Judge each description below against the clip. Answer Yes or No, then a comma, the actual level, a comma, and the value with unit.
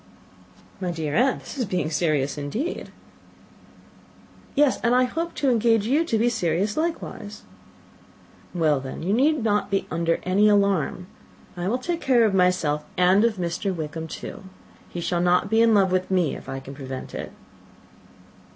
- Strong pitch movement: Yes, wide, 5.7 semitones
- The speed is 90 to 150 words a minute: No, average, 170 wpm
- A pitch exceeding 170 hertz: Yes, high, 190 Hz